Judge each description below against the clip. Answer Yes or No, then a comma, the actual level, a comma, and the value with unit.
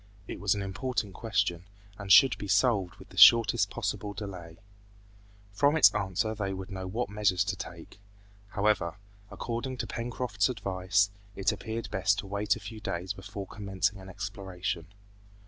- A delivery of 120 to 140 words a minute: No, average, 160 wpm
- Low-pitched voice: Yes, low, 100 Hz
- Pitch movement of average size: No, narrow, 2.3 semitones